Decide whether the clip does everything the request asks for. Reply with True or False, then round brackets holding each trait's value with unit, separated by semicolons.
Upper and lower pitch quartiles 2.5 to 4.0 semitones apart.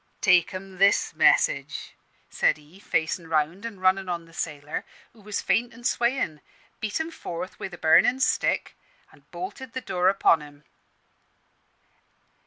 False (5.5 semitones)